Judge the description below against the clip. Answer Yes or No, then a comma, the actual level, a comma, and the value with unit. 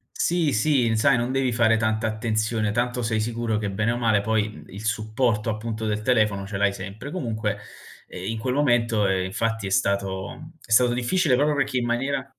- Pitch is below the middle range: Yes, low, 115 Hz